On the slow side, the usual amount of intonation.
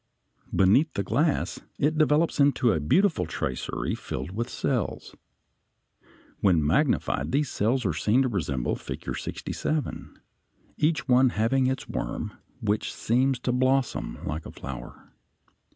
No: slow, 130 wpm; wide, 7.0 semitones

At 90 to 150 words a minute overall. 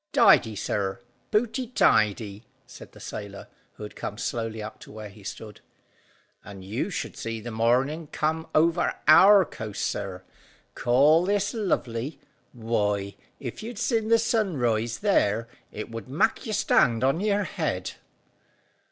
Yes: average, 145 wpm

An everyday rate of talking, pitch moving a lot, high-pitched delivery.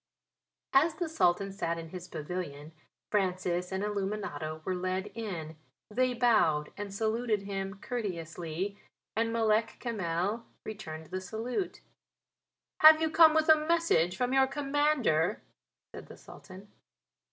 No: slow, 130 wpm; wide, 5.7 semitones; high, 205 Hz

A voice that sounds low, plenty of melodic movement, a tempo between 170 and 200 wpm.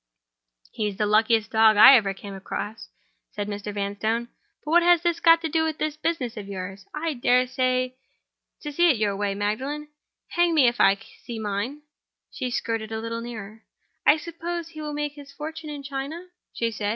No: high, 245 Hz; wide, 6.2 semitones; average, 190 wpm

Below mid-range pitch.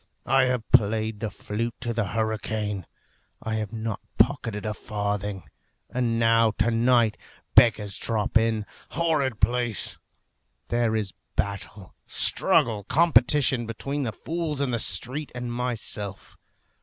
Yes: low, 115 Hz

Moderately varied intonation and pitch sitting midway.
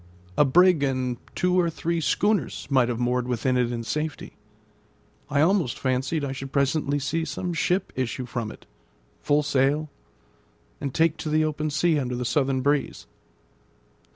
Yes: average, 3.5 semitones; medium, 145 Hz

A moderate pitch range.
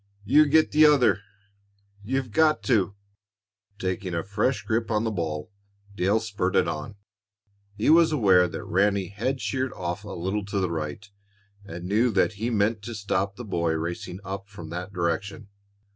Yes: average, 4.0 semitones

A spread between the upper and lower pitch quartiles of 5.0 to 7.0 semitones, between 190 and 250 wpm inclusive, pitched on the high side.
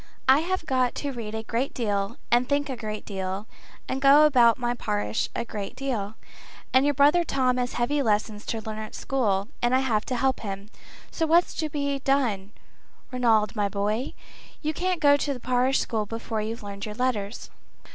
No: average, 4.3 semitones; average, 195 wpm; high, 240 Hz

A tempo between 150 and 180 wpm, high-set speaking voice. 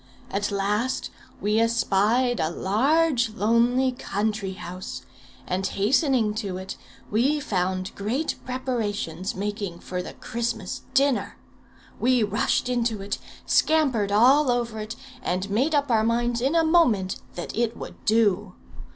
No: slow, 135 wpm; high, 225 Hz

